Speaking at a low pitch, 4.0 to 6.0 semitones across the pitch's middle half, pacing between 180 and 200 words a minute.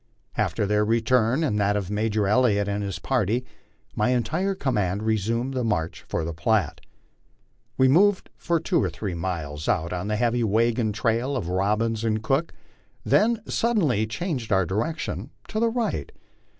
No: low, 110 Hz; average, 4.5 semitones; average, 165 wpm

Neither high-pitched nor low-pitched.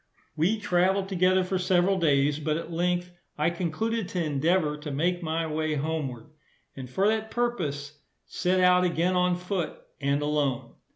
Yes: medium, 170 Hz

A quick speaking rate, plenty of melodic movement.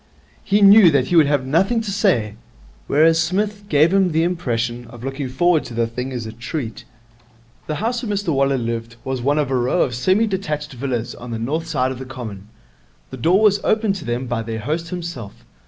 Yes: fast, 215 wpm; wide, 6.8 semitones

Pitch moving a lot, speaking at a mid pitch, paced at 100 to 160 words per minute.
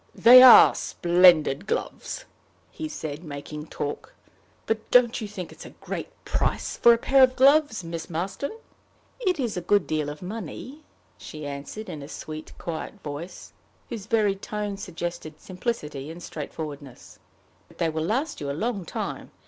Yes: wide, 6.8 semitones; medium, 180 Hz; average, 155 wpm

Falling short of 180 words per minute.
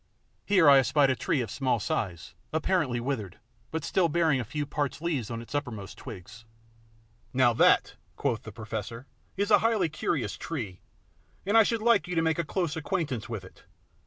No: average, 185 wpm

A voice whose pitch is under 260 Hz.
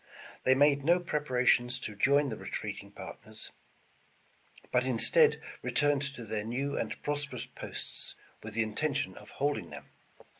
Yes: low, 135 Hz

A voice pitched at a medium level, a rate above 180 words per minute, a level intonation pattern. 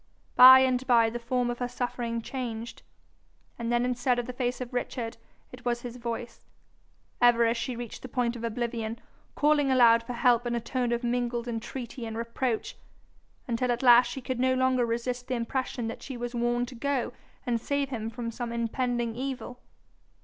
No: high, 240 Hz; average, 190 wpm; narrow, 1.3 semitones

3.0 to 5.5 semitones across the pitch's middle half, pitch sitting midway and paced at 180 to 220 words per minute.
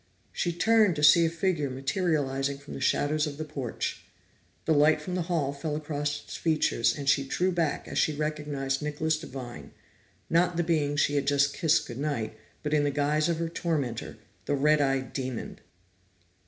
No: narrow, 2.4 semitones; medium, 150 Hz; average, 185 wpm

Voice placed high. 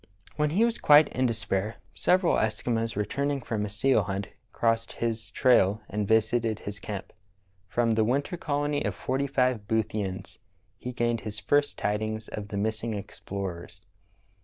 No: low, 110 Hz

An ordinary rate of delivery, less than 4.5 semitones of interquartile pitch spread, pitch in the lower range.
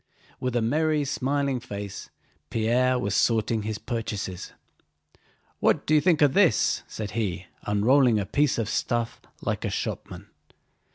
No: average, 145 wpm; average, 4.9 semitones; low, 120 Hz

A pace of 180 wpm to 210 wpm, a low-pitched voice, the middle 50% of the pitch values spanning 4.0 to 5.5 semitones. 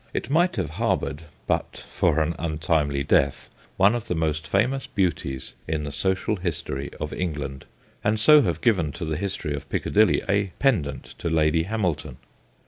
No: average, 165 wpm; very low, 85 Hz; average, 5.2 semitones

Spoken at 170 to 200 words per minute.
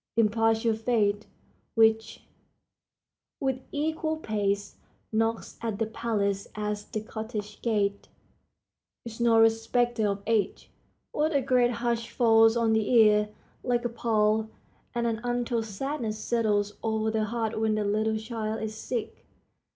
No: slow, 135 wpm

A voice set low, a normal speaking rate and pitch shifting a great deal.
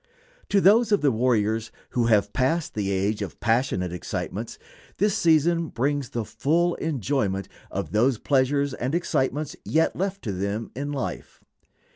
Yes: low, 130 Hz; average, 150 wpm; wide, 6.5 semitones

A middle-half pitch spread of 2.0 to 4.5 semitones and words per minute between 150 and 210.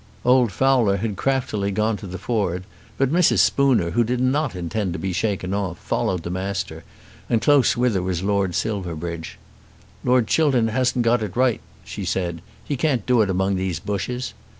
No: average, 5.2 semitones; average, 180 wpm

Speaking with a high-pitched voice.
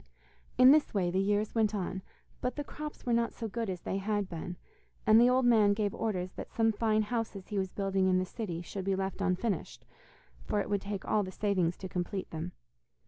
Yes: high, 205 Hz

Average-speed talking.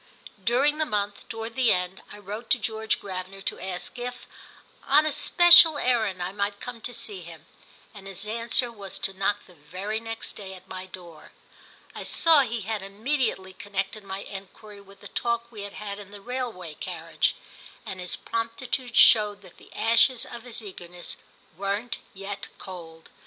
Yes: average, 175 wpm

